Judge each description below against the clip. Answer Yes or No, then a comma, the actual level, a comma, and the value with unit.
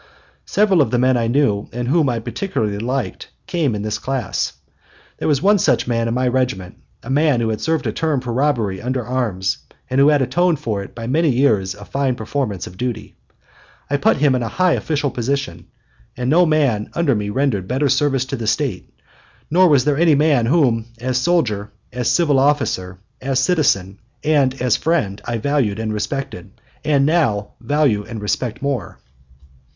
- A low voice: Yes, low, 130 Hz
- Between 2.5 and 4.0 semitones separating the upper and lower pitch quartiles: No, average, 4.6 semitones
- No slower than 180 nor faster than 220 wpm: Yes, average, 190 wpm